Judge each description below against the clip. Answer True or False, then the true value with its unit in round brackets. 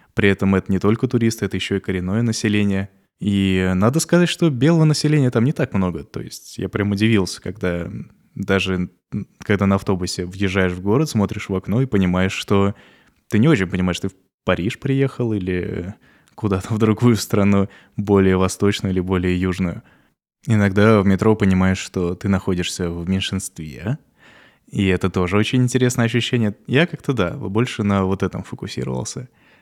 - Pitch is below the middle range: True (100 Hz)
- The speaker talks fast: True (165 wpm)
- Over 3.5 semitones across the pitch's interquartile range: False (2.8 semitones)